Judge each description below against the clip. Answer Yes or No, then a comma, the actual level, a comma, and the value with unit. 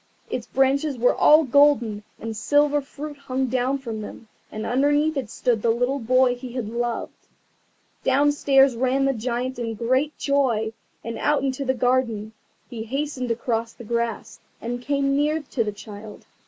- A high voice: Yes, very high, 255 Hz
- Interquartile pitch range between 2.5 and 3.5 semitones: Yes, average, 3.2 semitones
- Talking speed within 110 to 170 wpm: Yes, average, 165 wpm